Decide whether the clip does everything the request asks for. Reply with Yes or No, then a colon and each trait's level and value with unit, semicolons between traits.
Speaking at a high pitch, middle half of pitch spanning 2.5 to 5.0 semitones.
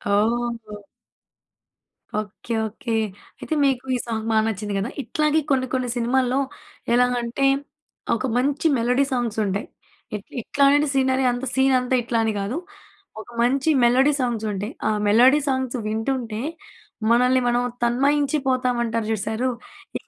Yes: high, 245 Hz; average, 2.9 semitones